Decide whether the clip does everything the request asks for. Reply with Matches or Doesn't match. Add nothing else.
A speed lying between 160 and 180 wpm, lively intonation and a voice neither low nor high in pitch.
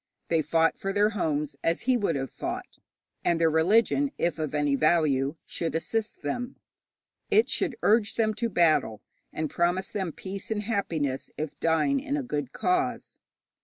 Matches